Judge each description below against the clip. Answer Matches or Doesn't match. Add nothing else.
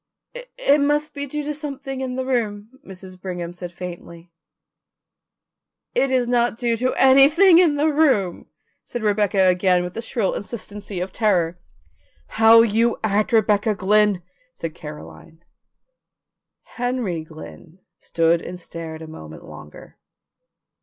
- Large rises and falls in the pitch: Matches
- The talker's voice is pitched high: Matches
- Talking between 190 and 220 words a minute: Doesn't match